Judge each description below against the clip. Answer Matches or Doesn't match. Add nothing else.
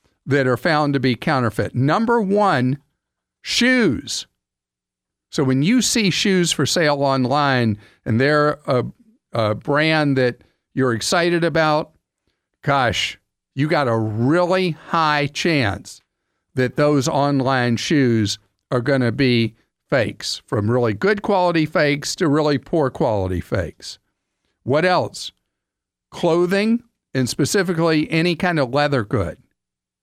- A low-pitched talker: Doesn't match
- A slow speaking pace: Matches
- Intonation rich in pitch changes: Matches